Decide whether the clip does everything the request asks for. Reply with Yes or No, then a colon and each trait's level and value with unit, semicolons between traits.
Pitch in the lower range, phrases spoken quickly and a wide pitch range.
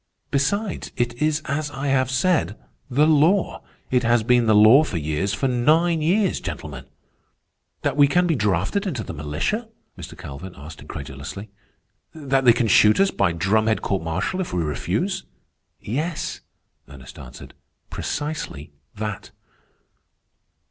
No: low, 125 Hz; average, 140 wpm; wide, 8.1 semitones